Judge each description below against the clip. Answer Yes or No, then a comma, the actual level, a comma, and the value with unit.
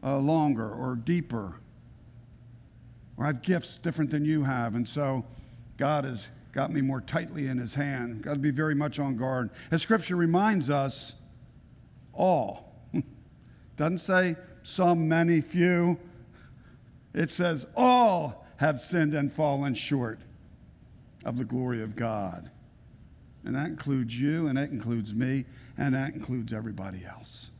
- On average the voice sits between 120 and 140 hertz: Yes, low, 135 Hz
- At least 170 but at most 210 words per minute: No, average, 145 wpm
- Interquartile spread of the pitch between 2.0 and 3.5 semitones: No, average, 4.6 semitones